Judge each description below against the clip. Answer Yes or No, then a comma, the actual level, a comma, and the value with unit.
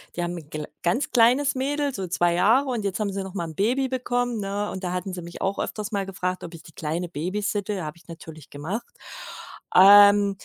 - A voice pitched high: Yes, high, 195 Hz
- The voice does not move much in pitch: No, average, 4.3 semitones